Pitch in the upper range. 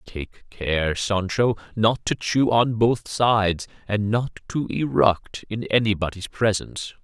No: low, 105 Hz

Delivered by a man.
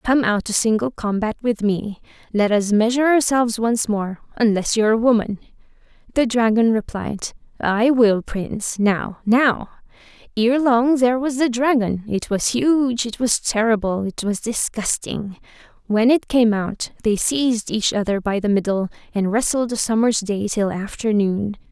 No: female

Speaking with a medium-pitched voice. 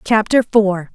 No: high, 205 Hz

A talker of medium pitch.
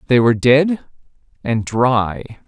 No: low, 125 Hz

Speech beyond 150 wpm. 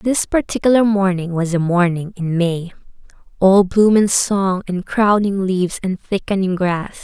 No: average, 145 wpm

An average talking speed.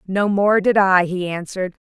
Yes: average, 195 wpm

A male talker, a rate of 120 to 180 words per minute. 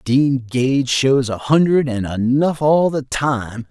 Yes: male; average, 160 wpm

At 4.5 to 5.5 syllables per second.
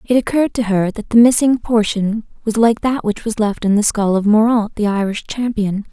Yes: 5.2 syllables/s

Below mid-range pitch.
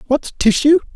No: very high, 265 Hz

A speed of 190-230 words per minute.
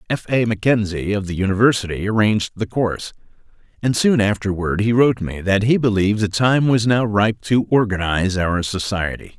No: average, 175 wpm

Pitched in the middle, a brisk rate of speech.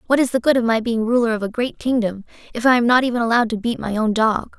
No: high, 230 Hz; fast, 300 wpm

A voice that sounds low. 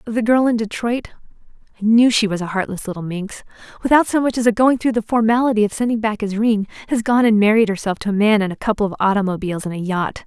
No: high, 215 Hz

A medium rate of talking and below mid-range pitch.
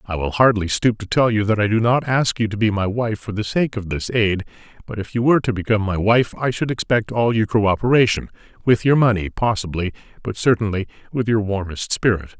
No: fast, 220 wpm; low, 110 Hz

